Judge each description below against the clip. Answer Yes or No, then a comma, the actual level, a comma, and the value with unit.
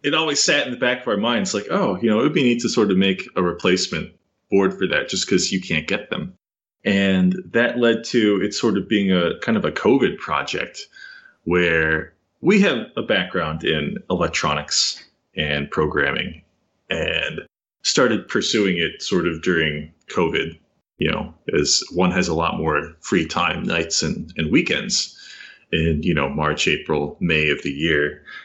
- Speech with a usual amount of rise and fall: No, wide, 7.6 semitones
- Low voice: Yes, low, 100 Hz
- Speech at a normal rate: Yes, average, 185 wpm